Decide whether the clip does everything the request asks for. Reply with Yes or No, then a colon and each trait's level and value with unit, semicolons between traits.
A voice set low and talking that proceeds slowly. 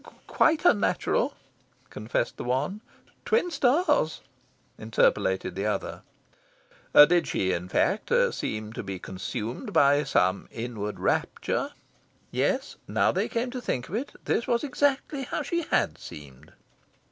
No: medium, 150 Hz; slow, 130 wpm